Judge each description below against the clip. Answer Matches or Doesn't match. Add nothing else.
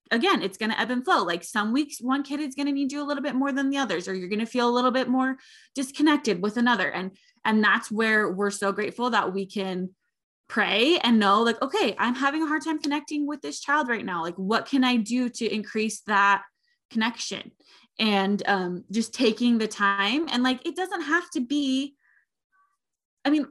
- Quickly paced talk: Matches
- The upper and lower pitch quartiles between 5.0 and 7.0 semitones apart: Matches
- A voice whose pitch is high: Matches